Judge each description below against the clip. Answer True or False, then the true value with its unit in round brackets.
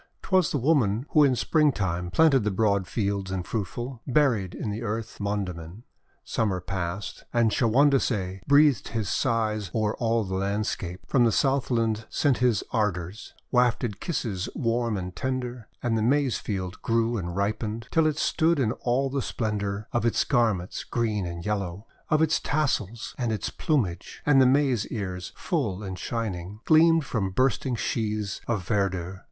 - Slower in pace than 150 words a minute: False (165 wpm)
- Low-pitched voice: True (110 Hz)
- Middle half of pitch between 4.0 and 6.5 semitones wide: True (4.5 semitones)